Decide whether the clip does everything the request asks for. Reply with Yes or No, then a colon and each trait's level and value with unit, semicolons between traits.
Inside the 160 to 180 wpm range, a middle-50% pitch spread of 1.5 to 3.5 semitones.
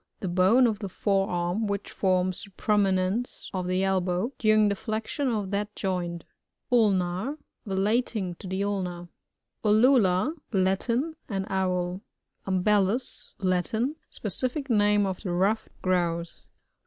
No: average, 150 wpm; average, 2.9 semitones